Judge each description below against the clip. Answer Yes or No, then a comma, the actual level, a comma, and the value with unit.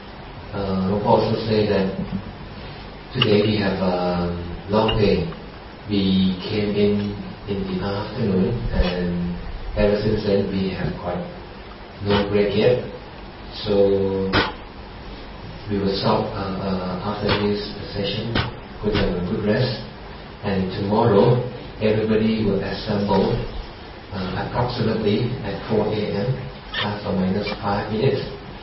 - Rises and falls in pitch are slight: Yes, narrow, 1.7 semitones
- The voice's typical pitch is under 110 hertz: Yes, low, 100 Hz